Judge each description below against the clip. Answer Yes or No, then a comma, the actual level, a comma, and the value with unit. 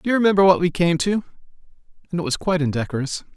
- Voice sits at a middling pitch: Yes, medium, 170 Hz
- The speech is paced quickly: Yes, fast, 215 wpm